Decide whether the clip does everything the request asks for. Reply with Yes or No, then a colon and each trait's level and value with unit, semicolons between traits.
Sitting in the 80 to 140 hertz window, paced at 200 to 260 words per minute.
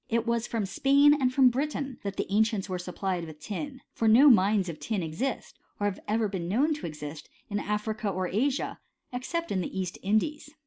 No: high, 215 Hz; fast, 205 wpm